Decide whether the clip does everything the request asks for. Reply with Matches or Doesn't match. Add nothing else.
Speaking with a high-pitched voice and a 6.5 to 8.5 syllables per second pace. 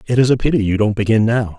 Doesn't match